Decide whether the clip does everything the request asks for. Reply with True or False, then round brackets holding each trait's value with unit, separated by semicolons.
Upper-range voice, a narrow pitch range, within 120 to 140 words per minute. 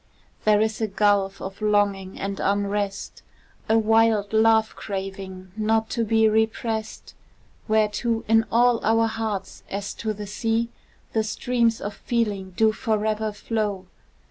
True (215 Hz; 1.8 semitones; 135 wpm)